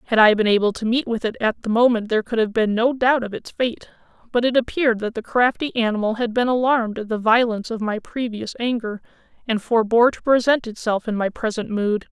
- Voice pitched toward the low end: No, high, 230 Hz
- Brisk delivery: Yes, fast, 225 wpm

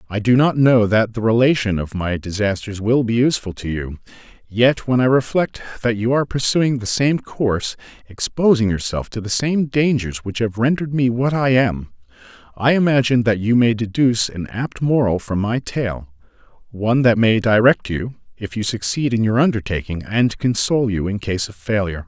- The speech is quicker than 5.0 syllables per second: Yes, 5.2 syllables/s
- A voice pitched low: Yes, low, 115 Hz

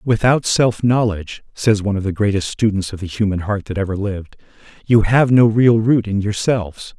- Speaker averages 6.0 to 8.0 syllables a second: No, 5.3 syllables/s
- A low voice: Yes, low, 105 Hz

